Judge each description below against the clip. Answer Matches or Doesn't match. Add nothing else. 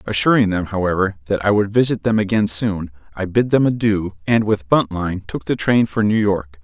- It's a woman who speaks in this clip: Doesn't match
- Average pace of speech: Doesn't match